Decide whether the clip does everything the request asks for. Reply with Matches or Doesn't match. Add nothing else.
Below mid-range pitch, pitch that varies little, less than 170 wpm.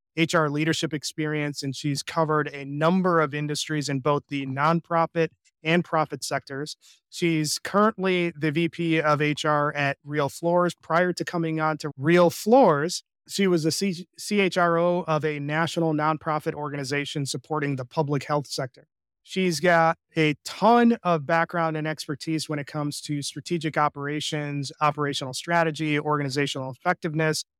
Doesn't match